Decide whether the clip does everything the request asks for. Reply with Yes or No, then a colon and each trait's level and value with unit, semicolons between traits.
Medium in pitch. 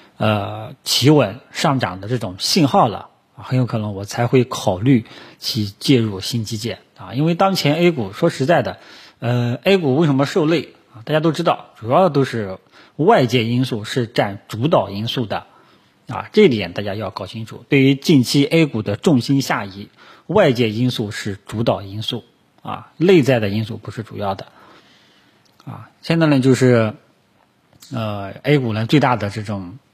No: low, 125 Hz